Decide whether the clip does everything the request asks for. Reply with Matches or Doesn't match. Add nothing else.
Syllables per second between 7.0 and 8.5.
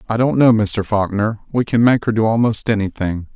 Doesn't match